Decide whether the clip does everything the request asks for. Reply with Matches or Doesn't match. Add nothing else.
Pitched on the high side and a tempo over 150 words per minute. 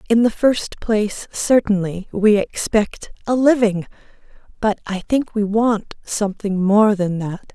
Doesn't match